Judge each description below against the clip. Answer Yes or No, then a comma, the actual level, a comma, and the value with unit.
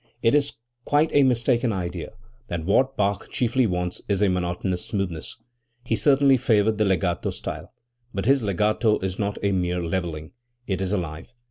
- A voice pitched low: Yes, low, 100 Hz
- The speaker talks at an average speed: Yes, average, 165 wpm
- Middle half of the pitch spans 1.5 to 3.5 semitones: No, average, 4.9 semitones